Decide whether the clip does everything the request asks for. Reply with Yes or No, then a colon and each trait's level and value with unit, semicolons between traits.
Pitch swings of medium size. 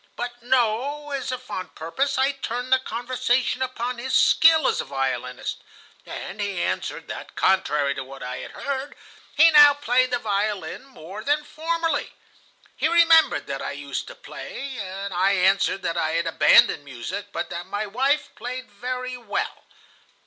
No: wide, 6.1 semitones